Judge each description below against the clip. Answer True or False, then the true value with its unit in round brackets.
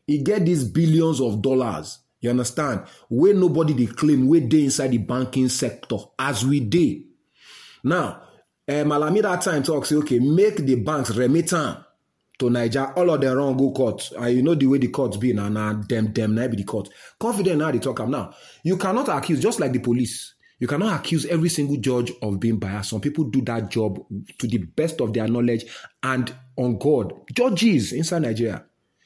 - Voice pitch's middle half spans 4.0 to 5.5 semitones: True (4.5 semitones)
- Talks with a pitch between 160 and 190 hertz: False (135 Hz)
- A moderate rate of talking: True (190 wpm)